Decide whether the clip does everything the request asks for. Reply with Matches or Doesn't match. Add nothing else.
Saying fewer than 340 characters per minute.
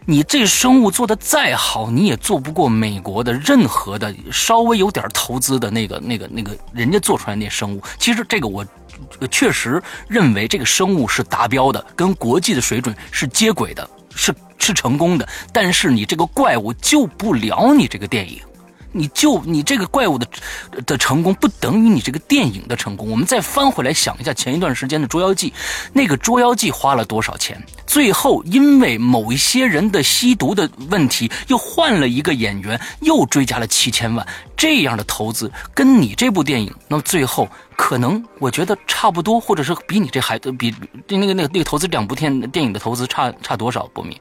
Matches